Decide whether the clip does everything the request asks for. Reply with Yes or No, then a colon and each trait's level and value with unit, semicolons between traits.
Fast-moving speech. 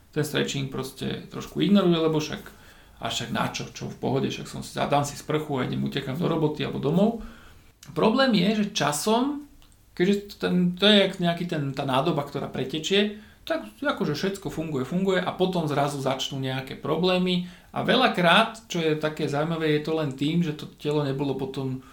Yes: fast, 180 wpm